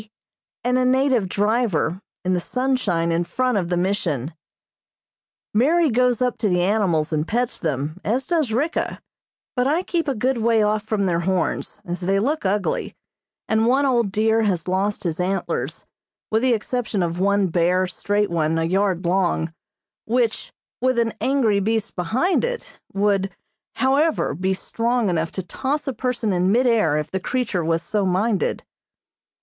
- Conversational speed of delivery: Yes, average, 165 wpm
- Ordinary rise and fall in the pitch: No, wide, 5.7 semitones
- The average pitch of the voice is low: No, high, 205 Hz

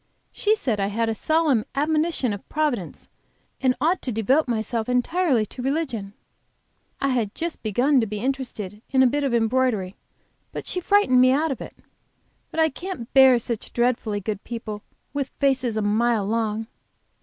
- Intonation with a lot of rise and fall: No, average, 4.3 semitones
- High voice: Yes, very high, 250 Hz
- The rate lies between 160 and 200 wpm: Yes, average, 170 wpm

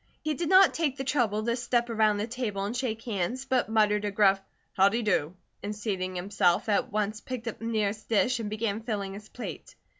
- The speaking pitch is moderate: No, high, 215 Hz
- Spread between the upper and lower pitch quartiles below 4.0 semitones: Yes, average, 2.9 semitones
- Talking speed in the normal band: No, fast, 210 wpm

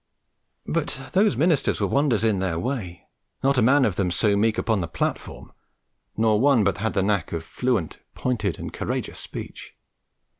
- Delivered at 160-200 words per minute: Yes, average, 175 wpm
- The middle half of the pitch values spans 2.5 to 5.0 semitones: No, wide, 5.5 semitones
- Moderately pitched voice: No, low, 110 Hz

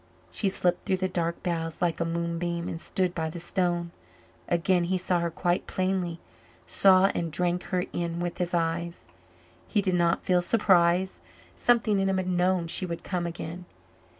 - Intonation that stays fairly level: Yes, narrow, 1.6 semitones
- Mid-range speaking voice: Yes, medium, 175 Hz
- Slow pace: No, average, 180 wpm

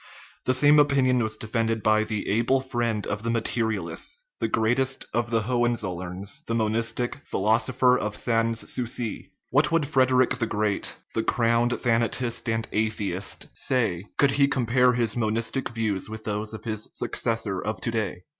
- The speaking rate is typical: Yes, average, 165 wpm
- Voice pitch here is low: Yes, low, 115 Hz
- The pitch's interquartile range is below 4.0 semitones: Yes, narrow, 2.6 semitones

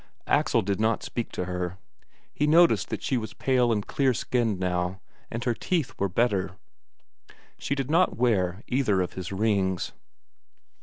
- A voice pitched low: Yes, low, 110 Hz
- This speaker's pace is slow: No, average, 160 wpm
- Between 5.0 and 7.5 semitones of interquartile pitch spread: Yes, average, 5.3 semitones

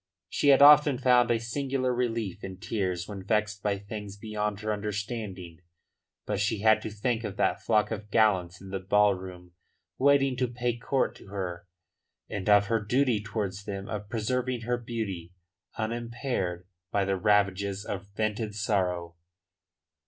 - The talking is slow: No, average, 160 wpm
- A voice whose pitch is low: Yes, low, 105 Hz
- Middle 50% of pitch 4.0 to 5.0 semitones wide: No, average, 3.1 semitones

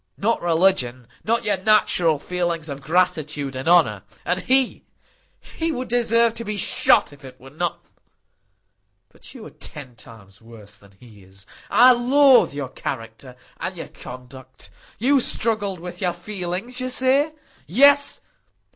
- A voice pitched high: No, medium, 175 Hz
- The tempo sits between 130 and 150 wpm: Yes, average, 140 wpm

